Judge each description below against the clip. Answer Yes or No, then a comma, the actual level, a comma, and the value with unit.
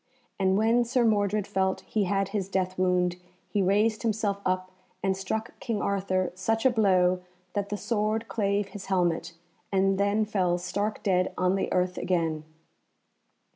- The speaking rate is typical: Yes, average, 160 wpm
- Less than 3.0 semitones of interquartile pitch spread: Yes, narrow, 2.4 semitones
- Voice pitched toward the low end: No, high, 195 Hz